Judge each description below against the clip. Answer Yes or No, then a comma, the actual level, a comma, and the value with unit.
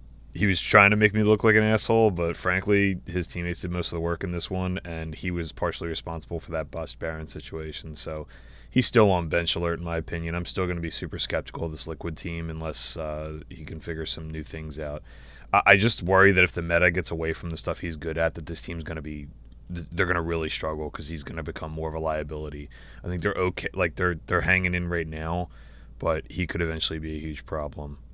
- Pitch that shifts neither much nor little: No, narrow, 2.3 semitones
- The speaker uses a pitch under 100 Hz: Yes, very low, 85 Hz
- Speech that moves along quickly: Yes, fast, 245 wpm